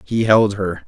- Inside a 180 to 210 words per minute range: Yes, fast, 205 wpm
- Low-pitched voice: Yes, low, 100 Hz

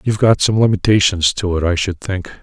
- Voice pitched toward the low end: Yes, very low, 95 Hz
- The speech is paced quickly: Yes, fast, 225 wpm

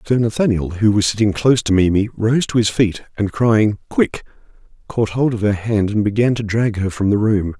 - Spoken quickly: Yes, fast, 220 wpm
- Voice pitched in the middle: No, low, 105 Hz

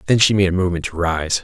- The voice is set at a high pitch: No, very low, 90 Hz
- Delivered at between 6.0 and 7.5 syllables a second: Yes, 7.2 syllables/s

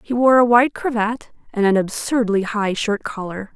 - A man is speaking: No, female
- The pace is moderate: Yes, average, 185 wpm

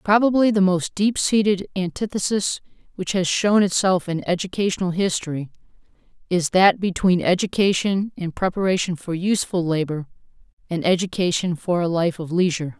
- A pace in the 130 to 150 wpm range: Yes, slow, 135 wpm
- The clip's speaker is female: Yes, female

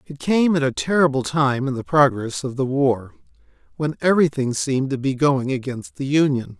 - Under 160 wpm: No, average, 190 wpm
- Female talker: No, male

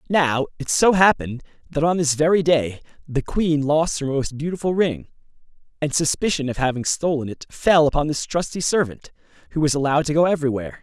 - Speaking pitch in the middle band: Yes, medium, 150 Hz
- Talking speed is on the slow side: No, average, 185 wpm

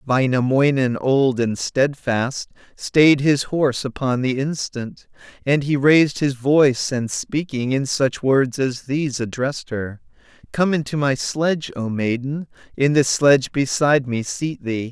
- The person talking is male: Yes, male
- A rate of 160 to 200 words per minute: No, average, 150 wpm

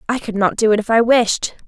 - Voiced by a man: No, female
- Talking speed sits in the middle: No, fast, 285 wpm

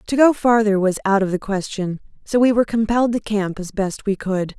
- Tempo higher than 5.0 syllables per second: Yes, 5.6 syllables/s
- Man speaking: No, female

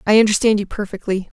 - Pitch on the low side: No, high, 205 Hz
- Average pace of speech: Yes, average, 170 wpm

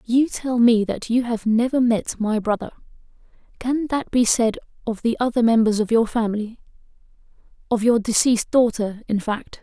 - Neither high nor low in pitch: No, high, 230 Hz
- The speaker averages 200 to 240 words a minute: No, average, 160 wpm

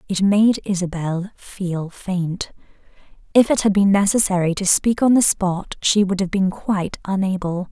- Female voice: Yes, female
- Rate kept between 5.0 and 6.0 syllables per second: No, 4.4 syllables/s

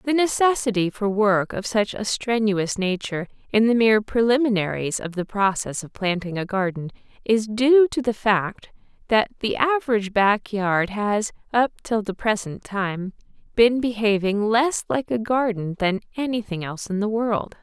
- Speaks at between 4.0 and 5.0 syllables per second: Yes, 4.7 syllables/s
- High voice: Yes, high, 215 Hz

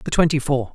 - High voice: No, medium, 140 Hz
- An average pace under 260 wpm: Yes, fast, 240 wpm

